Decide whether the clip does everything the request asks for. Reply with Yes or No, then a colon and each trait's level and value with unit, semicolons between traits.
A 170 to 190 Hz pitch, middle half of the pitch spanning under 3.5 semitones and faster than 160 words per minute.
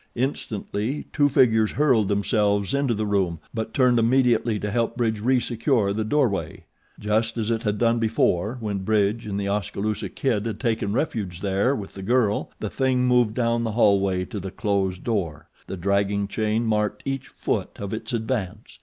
No: low, 110 Hz; average, 2.8 semitones; average, 175 wpm